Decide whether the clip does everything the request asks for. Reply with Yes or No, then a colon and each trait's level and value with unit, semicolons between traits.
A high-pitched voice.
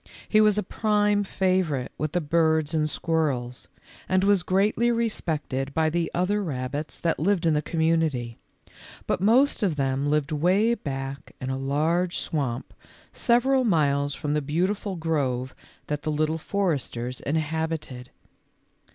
No: medium, 160 Hz